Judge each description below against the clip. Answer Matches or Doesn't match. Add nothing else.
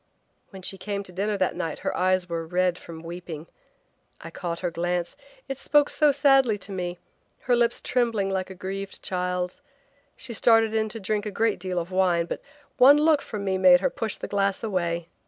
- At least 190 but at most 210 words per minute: Matches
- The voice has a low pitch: Doesn't match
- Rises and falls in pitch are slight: Doesn't match